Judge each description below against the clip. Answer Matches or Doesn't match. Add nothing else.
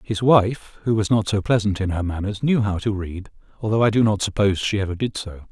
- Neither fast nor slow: Doesn't match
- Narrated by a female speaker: Doesn't match